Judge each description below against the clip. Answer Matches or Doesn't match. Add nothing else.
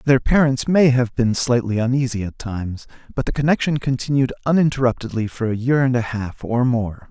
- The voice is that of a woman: Doesn't match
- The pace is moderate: Matches